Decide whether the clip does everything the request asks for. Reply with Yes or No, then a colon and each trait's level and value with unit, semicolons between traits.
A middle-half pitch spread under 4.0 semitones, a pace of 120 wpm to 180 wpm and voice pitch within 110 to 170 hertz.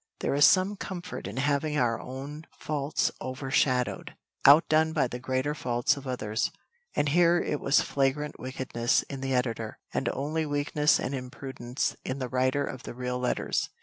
Yes: average, 2.7 semitones; average, 165 wpm; low, 135 Hz